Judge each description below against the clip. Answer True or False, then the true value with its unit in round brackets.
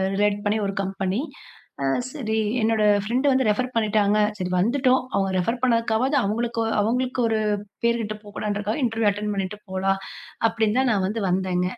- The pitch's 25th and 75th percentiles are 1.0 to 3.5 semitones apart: True (2.8 semitones)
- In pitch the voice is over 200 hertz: True (215 Hz)